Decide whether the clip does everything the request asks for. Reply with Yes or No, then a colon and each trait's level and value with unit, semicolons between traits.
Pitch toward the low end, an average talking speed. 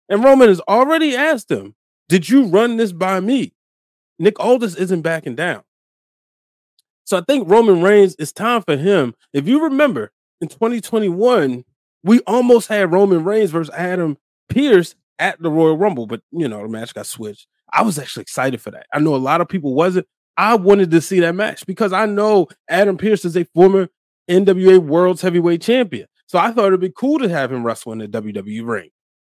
No: medium, 185 Hz; average, 195 wpm